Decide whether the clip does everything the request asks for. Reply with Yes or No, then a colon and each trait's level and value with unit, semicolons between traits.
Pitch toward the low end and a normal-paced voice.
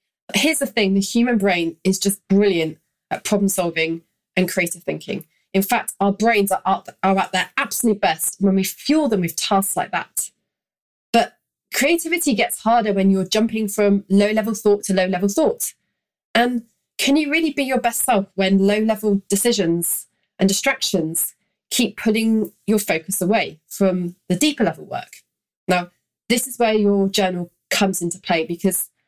No: high, 200 Hz; average, 170 wpm